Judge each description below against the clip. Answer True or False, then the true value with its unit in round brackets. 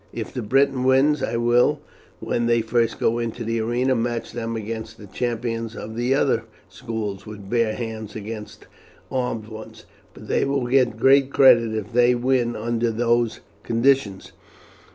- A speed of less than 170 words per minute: True (160 wpm)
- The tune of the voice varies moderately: False (1.8 semitones)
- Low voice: True (115 Hz)